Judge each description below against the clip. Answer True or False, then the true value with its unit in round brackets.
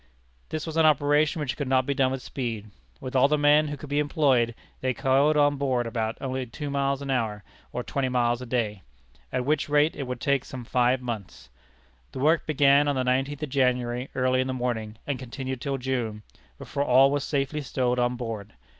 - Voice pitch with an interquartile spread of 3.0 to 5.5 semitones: False (2.6 semitones)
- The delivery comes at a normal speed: False (210 wpm)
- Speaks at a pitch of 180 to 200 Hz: False (130 Hz)